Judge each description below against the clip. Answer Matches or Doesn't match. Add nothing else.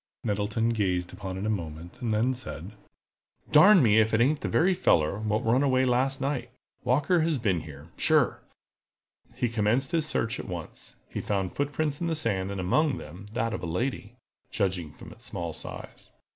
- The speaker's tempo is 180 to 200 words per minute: Matches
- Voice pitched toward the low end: Matches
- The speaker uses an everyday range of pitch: Doesn't match